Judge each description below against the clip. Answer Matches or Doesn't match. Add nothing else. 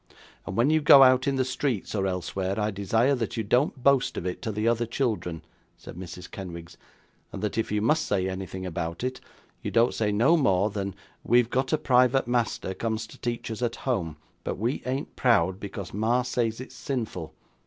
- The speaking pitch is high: Doesn't match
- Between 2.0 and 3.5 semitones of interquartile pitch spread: Doesn't match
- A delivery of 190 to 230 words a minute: Matches